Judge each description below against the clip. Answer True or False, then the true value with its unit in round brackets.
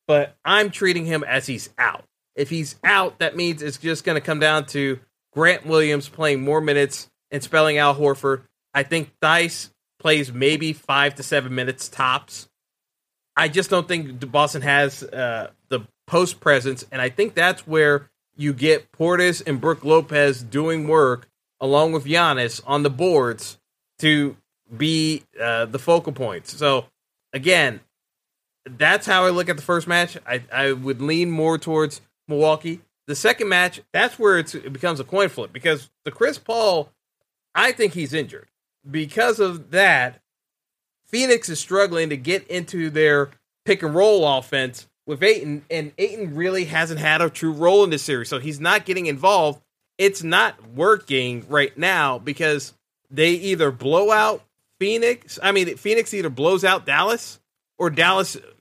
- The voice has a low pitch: False (155 Hz)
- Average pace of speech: True (165 wpm)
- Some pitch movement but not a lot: True (3.9 semitones)